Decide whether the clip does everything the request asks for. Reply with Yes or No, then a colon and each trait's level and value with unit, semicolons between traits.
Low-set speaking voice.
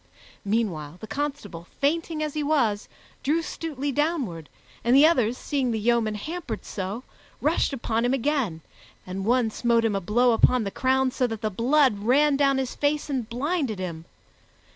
No: high, 245 Hz